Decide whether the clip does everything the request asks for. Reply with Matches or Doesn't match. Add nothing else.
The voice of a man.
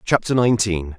Matches